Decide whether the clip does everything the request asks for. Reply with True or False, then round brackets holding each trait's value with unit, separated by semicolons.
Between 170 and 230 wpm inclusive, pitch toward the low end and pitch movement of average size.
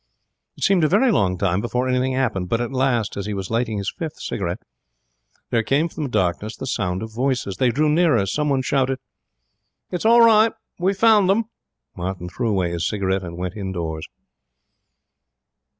False (180 wpm; 120 Hz; 7.7 semitones)